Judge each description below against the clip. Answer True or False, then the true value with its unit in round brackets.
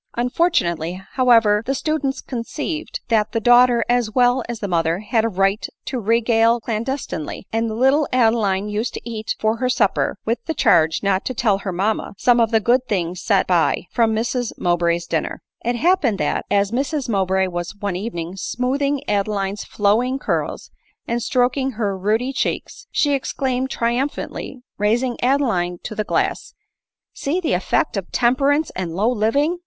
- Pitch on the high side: True (230 Hz)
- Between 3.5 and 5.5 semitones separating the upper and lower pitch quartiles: True (4.2 semitones)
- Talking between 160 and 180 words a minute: True (170 wpm)